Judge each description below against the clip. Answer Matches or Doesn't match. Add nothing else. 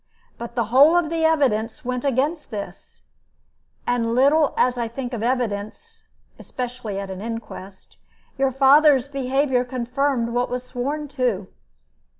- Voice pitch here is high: Matches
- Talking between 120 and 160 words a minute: Matches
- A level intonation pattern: Doesn't match